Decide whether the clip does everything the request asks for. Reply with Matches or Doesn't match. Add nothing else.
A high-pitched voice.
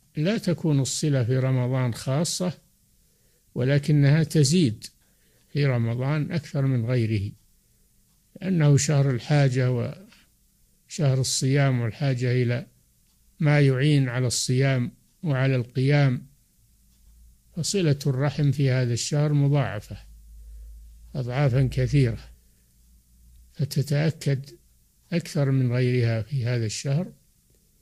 Doesn't match